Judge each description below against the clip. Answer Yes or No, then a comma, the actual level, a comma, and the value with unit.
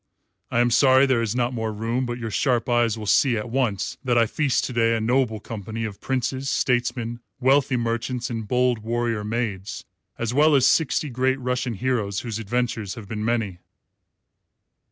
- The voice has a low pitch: Yes, low, 120 Hz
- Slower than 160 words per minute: No, average, 180 wpm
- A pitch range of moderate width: No, narrow, 2.2 semitones